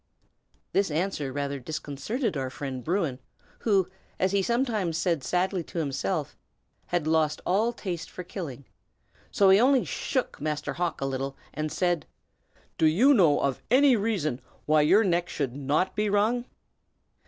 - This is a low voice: No, medium, 175 Hz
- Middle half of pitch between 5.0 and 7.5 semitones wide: Yes, wide, 5.6 semitones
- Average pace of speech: Yes, average, 155 wpm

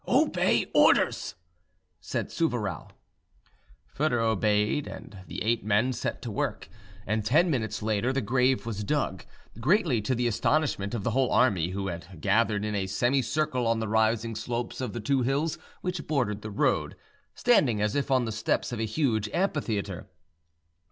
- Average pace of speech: Yes, average, 165 wpm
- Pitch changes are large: No, average, 4.1 semitones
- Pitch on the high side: No, low, 115 Hz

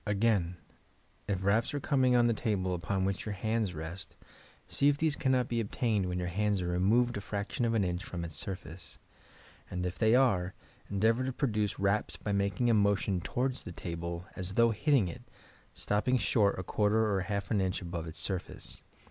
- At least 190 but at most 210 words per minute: Yes, average, 200 wpm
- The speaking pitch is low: Yes, low, 100 Hz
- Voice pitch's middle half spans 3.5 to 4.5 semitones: Yes, average, 4.0 semitones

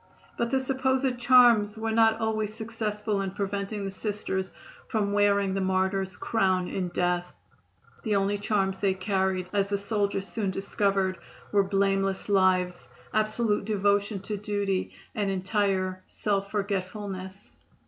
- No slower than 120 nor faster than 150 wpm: Yes, slow, 135 wpm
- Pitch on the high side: Yes, high, 200 Hz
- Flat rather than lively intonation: Yes, narrow, 2.0 semitones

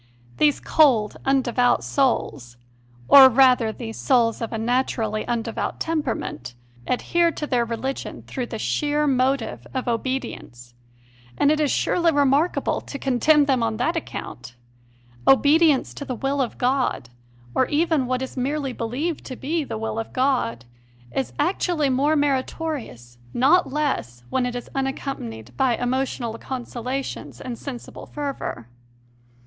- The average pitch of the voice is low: No, very high, 260 Hz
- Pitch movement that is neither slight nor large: Yes, average, 3.7 semitones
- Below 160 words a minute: Yes, average, 145 wpm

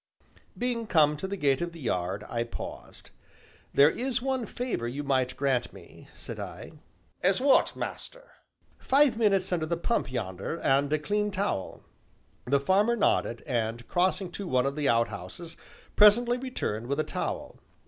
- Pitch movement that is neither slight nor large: No, wide, 8.6 semitones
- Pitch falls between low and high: Yes, medium, 165 Hz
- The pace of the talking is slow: No, average, 160 wpm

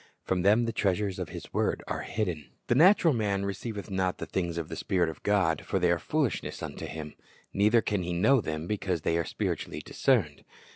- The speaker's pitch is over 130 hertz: No, very low, 95 Hz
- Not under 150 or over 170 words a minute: No, fast, 205 wpm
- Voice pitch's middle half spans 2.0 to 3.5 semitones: No, average, 3.9 semitones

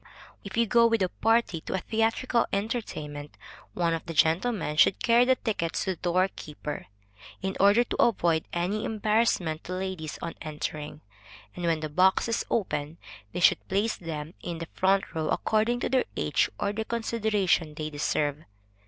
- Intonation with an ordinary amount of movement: No, wide, 5.7 semitones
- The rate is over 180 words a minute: No, average, 175 wpm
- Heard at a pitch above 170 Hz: Yes, medium, 185 Hz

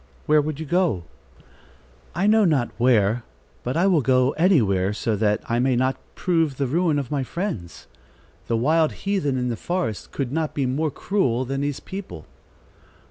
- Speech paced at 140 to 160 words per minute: No, average, 175 wpm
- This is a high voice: No, low, 135 Hz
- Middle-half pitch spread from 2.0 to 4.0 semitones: No, wide, 5.4 semitones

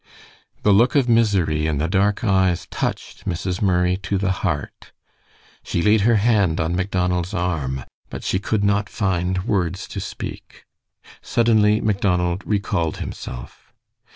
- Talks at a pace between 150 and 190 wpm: No, average, 140 wpm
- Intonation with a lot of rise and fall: No, average, 2.9 semitones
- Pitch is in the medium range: No, very low, 95 Hz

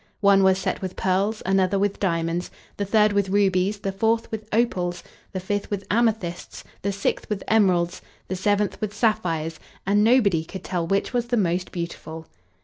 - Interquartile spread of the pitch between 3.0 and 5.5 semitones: No, narrow, 2.6 semitones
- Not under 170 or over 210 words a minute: Yes, average, 175 wpm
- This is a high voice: Yes, high, 195 Hz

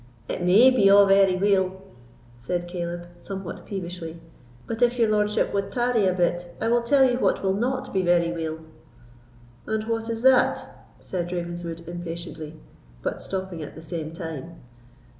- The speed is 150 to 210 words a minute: Yes, average, 160 wpm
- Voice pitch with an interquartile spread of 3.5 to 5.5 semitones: Yes, average, 4.0 semitones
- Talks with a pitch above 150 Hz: Yes, medium, 185 Hz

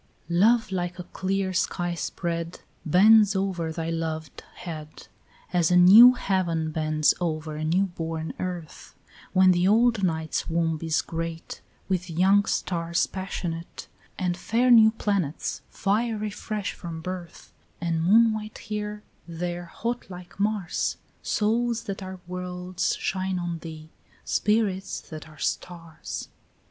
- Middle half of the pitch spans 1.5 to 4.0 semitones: Yes, average, 3.3 semitones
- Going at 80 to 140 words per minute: Yes, slow, 135 wpm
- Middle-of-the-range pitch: Yes, medium, 180 Hz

